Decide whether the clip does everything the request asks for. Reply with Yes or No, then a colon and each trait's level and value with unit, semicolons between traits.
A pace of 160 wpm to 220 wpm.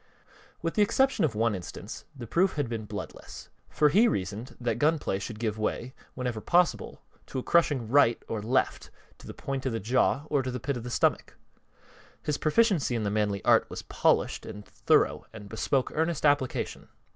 Yes: average, 190 wpm